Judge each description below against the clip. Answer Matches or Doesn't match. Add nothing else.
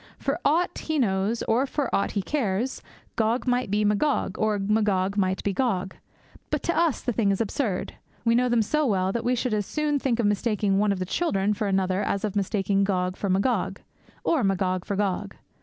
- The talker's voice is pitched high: Matches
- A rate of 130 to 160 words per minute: Doesn't match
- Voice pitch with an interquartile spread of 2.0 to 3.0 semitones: Doesn't match